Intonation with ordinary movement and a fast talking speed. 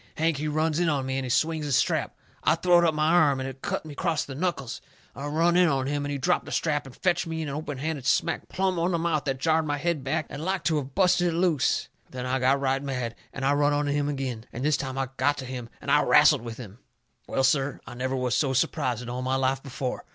Yes: average, 3.2 semitones; fast, 270 wpm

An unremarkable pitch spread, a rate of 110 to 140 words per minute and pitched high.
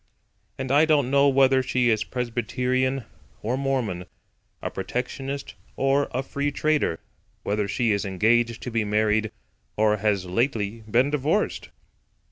No: average, 4.0 semitones; slow, 135 wpm; low, 125 Hz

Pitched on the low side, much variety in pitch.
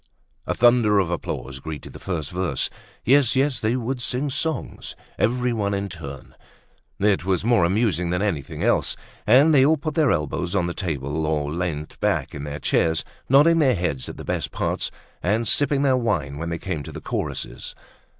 Yes: low, 100 Hz; wide, 7.6 semitones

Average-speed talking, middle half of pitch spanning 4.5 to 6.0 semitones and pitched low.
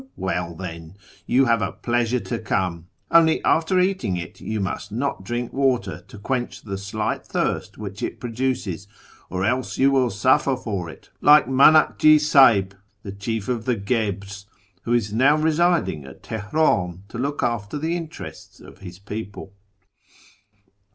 Yes: average, 155 wpm; wide, 5.4 semitones; low, 115 Hz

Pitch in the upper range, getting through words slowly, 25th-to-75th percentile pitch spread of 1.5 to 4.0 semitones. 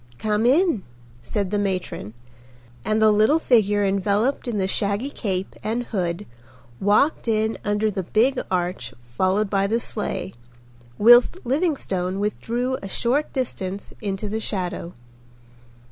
Yes: high, 210 Hz; slow, 130 wpm; average, 3.5 semitones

